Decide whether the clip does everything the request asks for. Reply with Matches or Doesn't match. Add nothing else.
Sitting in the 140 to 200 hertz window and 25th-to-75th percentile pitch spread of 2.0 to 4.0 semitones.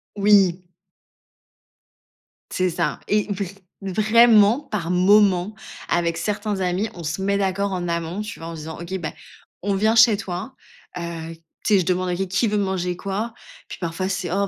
Matches